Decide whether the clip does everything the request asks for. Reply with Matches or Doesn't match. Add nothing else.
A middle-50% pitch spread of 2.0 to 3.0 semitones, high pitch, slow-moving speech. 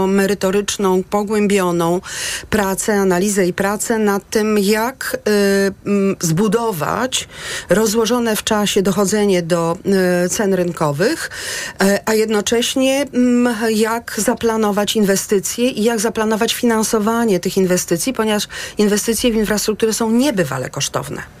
Matches